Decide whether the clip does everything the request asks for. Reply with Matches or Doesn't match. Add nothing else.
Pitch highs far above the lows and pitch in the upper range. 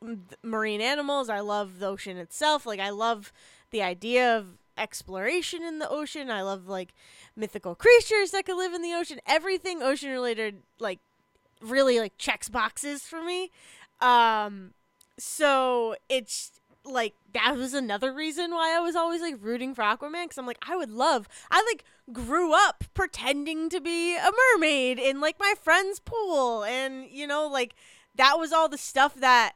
Matches